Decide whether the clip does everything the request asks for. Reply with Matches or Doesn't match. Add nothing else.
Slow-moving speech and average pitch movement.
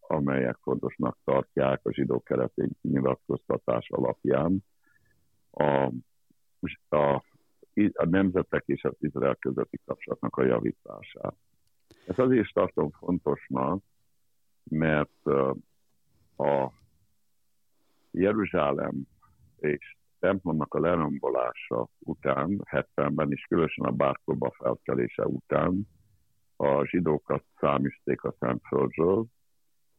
Doesn't match